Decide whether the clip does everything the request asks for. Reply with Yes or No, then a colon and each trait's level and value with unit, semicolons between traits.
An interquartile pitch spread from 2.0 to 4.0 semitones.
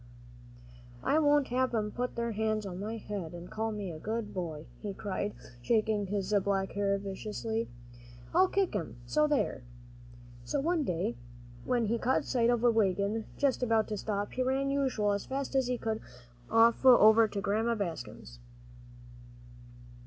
Yes: average, 3.5 semitones